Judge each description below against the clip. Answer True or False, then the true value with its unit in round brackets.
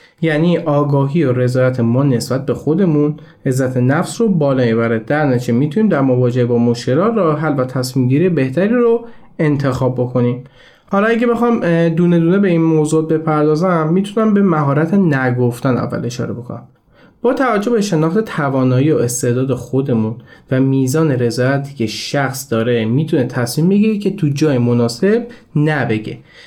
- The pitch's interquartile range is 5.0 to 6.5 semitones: True (5.3 semitones)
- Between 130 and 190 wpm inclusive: True (150 wpm)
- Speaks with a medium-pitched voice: True (145 Hz)